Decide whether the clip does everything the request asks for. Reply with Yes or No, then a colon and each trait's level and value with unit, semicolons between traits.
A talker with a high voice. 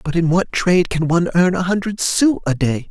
No: medium, 175 Hz